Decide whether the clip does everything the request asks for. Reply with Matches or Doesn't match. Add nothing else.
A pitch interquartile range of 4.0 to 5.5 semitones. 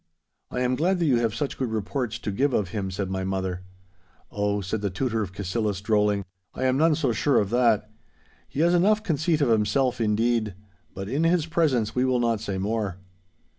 Matches